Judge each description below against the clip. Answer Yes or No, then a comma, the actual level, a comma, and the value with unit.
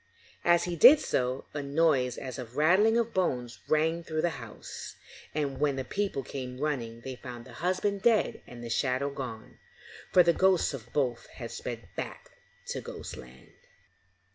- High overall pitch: No, medium, 140 Hz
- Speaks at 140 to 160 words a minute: No, average, 170 wpm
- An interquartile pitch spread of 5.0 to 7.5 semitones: Yes, wide, 5.5 semitones